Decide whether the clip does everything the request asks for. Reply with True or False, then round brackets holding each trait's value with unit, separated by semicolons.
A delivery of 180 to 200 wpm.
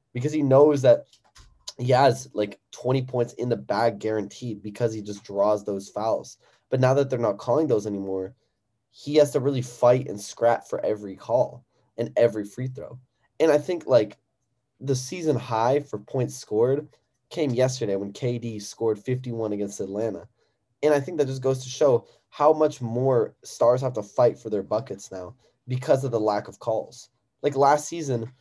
True (185 wpm)